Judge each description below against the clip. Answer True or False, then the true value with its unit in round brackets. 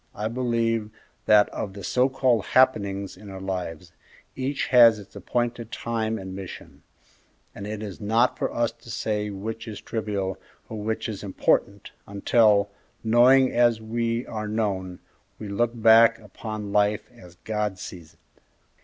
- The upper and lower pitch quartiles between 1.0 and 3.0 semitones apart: True (2.6 semitones)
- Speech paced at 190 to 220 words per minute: False (155 wpm)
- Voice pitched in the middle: False (110 Hz)